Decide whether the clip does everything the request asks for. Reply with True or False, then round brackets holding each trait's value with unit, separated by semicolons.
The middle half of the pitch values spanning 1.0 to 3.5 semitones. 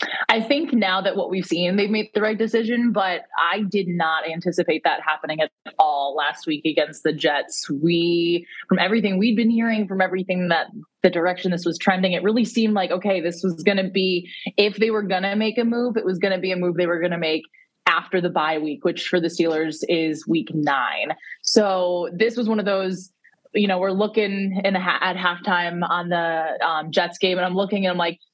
True (3.1 semitones)